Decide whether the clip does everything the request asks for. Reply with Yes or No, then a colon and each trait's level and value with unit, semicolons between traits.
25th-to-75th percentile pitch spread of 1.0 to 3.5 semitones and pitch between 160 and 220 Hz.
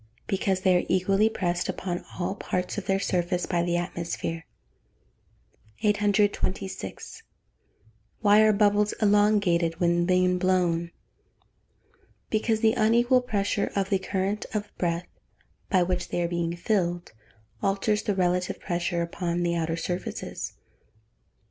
Yes: average, 2.9 semitones; medium, 185 Hz